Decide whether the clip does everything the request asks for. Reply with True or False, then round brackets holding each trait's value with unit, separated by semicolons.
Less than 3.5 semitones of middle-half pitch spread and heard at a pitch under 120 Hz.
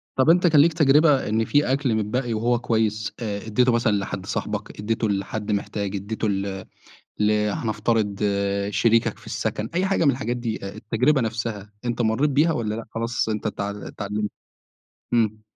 True (2.8 semitones; 110 Hz)